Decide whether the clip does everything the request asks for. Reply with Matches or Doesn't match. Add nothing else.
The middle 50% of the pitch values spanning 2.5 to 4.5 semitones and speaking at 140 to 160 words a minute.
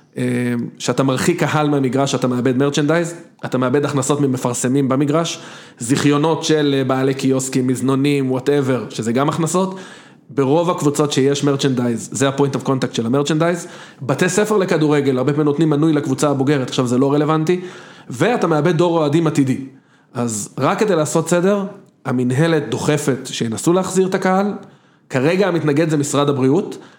Matches